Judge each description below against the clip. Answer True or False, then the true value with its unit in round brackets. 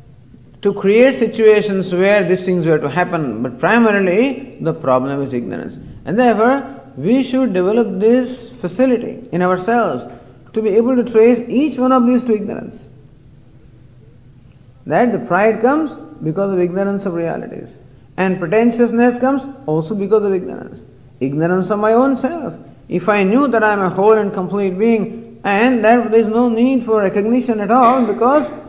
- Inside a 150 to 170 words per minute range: True (165 wpm)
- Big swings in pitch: True (6.1 semitones)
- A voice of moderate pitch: False (210 Hz)